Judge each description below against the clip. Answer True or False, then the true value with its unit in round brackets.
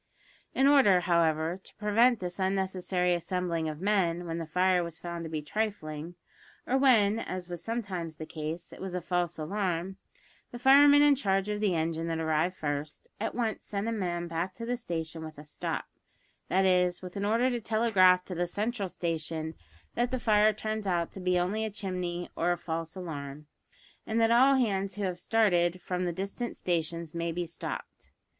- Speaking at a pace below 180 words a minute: False (190 wpm)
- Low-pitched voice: False (180 Hz)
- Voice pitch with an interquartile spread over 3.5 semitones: True (3.9 semitones)